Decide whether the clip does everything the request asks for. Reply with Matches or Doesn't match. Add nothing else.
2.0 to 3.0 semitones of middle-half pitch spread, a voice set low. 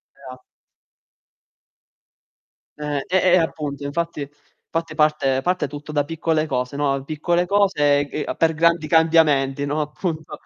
Doesn't match